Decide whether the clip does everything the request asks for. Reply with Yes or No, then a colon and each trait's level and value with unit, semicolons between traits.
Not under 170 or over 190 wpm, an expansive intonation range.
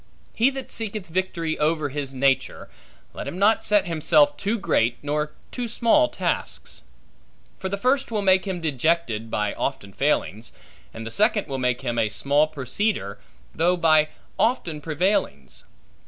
No: average, 155 wpm; wide, 6.6 semitones